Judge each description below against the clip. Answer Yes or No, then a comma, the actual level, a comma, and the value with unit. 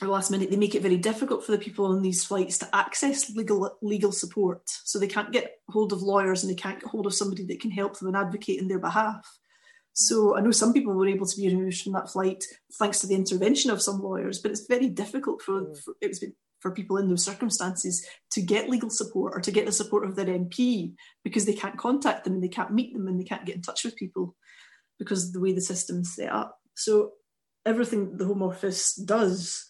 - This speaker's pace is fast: Yes, fast, 240 wpm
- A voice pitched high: Yes, high, 200 Hz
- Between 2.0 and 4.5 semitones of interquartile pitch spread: Yes, narrow, 2.5 semitones